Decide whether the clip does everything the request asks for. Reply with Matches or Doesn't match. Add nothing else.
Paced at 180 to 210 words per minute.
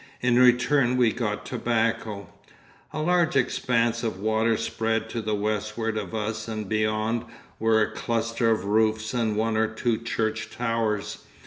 Doesn't match